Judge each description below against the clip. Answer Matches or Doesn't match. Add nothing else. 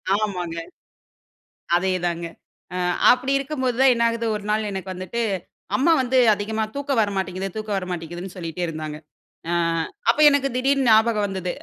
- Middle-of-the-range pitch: Doesn't match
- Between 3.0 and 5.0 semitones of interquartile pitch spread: Doesn't match